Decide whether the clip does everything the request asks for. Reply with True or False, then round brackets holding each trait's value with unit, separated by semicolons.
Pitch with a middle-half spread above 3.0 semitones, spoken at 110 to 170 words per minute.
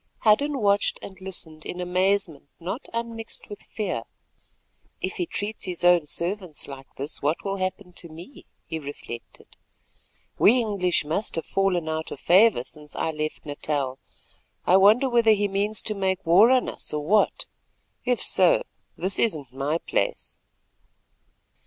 True (4.9 semitones; 150 wpm)